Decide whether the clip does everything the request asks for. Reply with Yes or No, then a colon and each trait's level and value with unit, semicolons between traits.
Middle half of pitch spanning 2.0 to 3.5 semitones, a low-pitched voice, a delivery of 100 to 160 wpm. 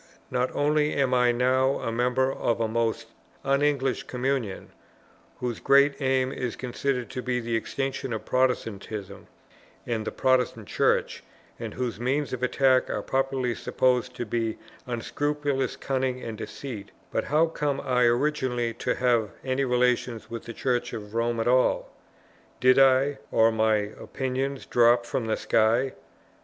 Yes: narrow, 2.4 semitones; low, 125 Hz; average, 150 wpm